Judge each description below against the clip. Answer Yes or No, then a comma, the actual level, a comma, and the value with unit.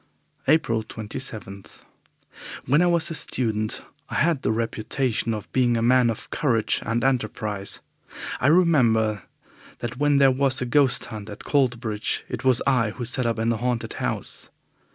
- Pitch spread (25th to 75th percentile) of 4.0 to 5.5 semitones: No, average, 3.3 semitones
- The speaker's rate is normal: Yes, average, 160 wpm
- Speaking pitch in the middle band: No, low, 120 Hz